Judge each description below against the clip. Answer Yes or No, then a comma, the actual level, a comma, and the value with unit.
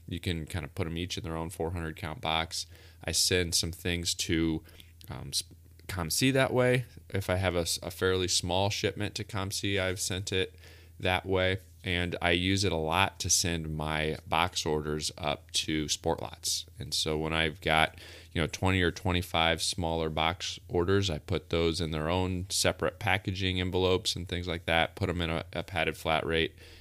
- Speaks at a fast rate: No, average, 190 wpm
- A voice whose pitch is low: Yes, very low, 85 Hz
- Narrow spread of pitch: Yes, narrow, 2.3 semitones